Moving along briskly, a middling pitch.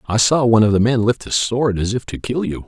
No: fast, 315 wpm; low, 115 Hz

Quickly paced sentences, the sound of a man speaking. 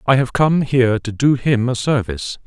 Yes: fast, 220 wpm; male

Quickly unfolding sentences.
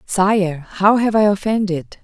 No: average, 145 wpm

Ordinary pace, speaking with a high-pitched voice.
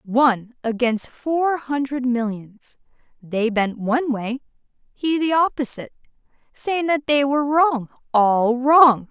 No: slow, 125 wpm; very high, 260 Hz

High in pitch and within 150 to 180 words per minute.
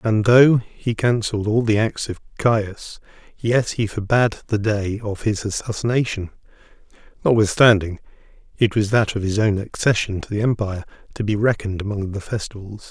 No: low, 105 Hz; average, 160 wpm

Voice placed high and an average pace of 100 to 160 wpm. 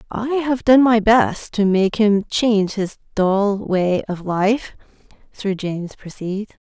Yes: high, 210 Hz; average, 155 wpm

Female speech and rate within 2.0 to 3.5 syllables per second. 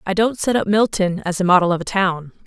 No: female; 5.8 syllables/s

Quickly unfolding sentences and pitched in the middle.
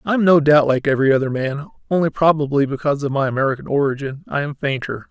Yes: fast, 210 wpm; medium, 145 Hz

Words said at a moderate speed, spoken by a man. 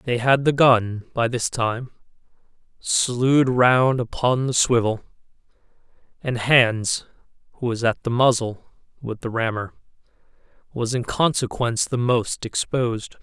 No: slow, 125 wpm; male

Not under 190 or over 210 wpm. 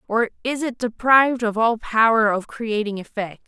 No: average, 175 wpm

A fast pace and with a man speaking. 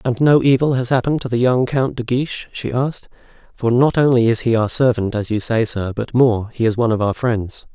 Yes: fast, 240 wpm; male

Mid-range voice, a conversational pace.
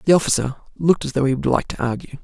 No: medium, 145 Hz; fast, 270 wpm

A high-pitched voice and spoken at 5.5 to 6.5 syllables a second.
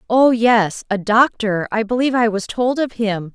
No: high, 225 Hz; 4.6 syllables/s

